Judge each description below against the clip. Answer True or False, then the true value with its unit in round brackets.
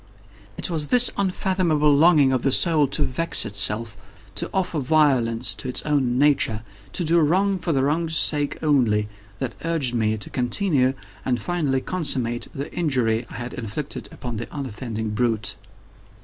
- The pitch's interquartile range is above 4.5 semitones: True (5.5 semitones)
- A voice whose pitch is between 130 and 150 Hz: True (135 Hz)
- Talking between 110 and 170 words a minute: True (150 wpm)